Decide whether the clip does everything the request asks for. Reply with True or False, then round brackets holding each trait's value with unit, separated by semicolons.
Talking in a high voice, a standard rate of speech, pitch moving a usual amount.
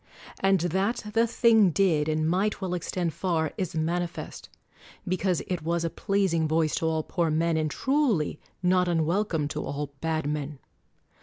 False (170 Hz; 160 wpm; 3.3 semitones)